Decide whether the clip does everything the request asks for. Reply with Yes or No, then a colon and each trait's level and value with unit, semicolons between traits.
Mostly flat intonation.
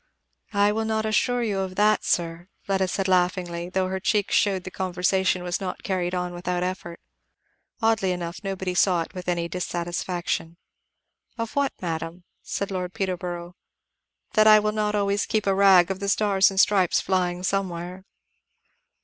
Yes: narrow, 2.1 semitones